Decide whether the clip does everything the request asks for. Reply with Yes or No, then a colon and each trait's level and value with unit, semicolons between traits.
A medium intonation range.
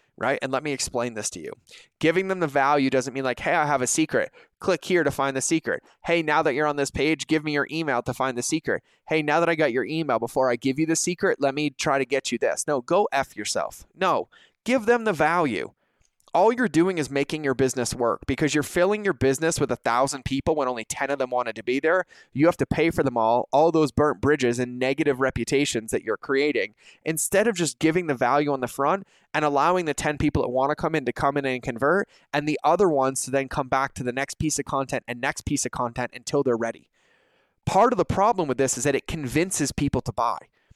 Yes: average, 3.2 semitones